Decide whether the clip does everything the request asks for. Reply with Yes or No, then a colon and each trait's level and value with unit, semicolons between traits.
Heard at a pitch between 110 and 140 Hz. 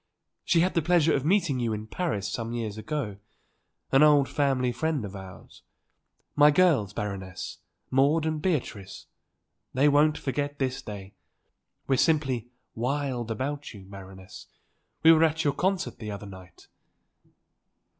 Yes: low, 135 Hz